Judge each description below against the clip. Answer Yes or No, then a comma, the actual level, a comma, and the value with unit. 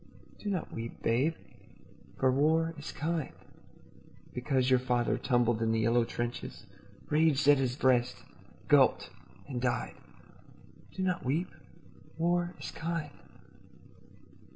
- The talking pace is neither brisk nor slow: No, slow, 120 wpm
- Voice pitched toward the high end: No, low, 135 Hz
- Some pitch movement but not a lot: Yes, average, 4.9 semitones